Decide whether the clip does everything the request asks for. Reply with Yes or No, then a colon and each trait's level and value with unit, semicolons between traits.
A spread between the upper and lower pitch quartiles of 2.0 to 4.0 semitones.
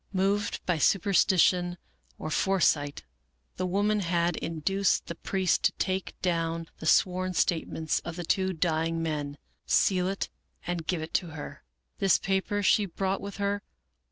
Yes: average, 2.7 semitones